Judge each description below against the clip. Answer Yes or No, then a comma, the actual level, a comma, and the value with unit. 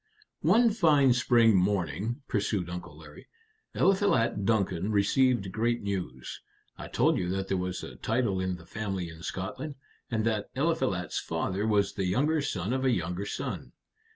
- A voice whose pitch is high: No, low, 100 Hz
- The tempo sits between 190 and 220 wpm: No, average, 155 wpm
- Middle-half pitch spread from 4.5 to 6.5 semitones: Yes, average, 4.8 semitones